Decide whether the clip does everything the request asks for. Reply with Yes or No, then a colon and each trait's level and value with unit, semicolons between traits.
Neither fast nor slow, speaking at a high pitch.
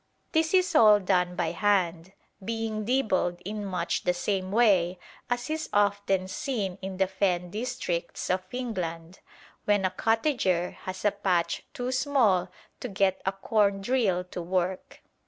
Yes: average, 145 wpm; high, 195 Hz